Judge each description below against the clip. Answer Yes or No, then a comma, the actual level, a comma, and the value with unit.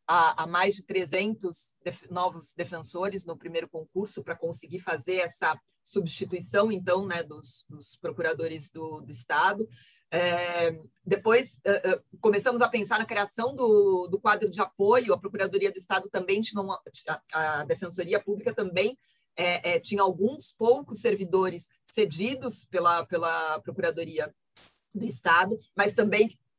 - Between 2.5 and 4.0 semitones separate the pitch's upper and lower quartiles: Yes, average, 3.7 semitones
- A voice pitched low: No, high, 190 Hz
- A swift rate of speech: No, average, 145 wpm